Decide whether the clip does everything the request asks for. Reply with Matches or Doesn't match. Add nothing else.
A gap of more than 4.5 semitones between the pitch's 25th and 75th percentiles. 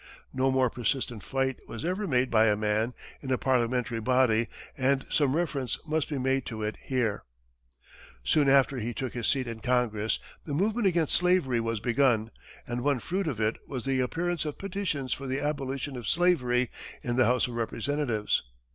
Doesn't match